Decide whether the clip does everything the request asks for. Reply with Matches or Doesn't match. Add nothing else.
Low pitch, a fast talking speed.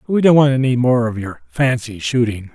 Matches